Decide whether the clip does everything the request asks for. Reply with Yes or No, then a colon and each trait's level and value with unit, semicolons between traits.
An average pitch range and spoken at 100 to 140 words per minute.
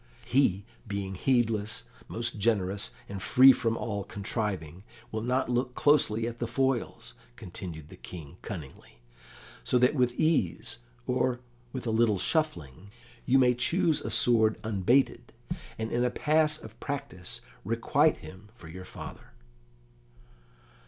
Yes: average, 4.3 semitones; slow, 135 wpm